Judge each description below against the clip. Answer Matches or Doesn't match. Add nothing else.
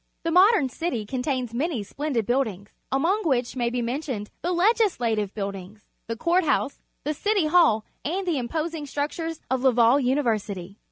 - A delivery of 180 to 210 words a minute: Doesn't match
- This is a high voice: Matches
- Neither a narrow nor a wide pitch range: Doesn't match